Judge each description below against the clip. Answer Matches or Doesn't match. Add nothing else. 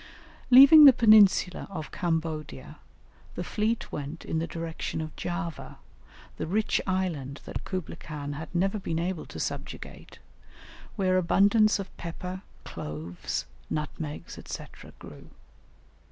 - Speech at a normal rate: Doesn't match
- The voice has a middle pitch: Matches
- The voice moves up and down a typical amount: Matches